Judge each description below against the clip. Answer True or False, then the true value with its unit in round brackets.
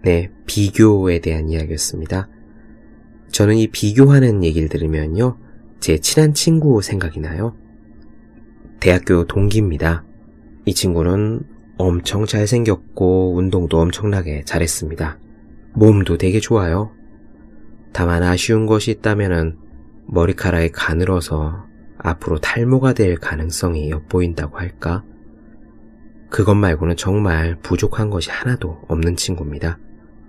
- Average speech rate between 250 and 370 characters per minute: True (265 characters per minute)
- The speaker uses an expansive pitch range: False (5.0 semitones)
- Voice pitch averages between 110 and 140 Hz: False (95 Hz)